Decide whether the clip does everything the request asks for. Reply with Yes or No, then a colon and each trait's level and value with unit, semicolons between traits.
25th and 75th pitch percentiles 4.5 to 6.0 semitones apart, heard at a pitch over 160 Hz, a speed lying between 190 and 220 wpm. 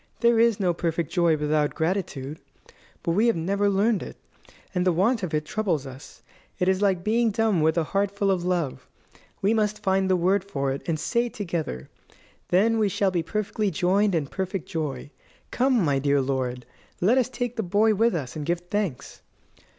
Yes: average, 4.8 semitones; medium, 185 Hz; average, 195 wpm